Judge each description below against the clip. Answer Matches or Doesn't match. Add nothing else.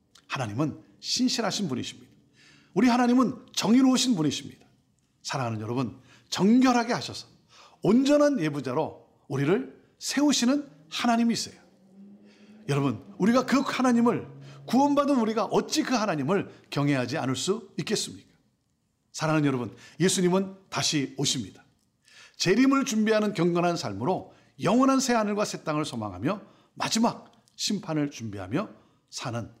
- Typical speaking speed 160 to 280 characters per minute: Doesn't match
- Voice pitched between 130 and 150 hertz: Doesn't match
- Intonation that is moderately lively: Doesn't match